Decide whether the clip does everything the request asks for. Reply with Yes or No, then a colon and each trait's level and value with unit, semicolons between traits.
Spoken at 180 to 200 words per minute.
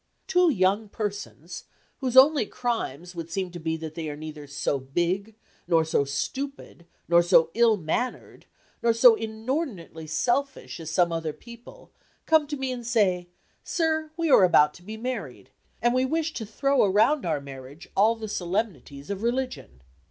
No: average, 165 wpm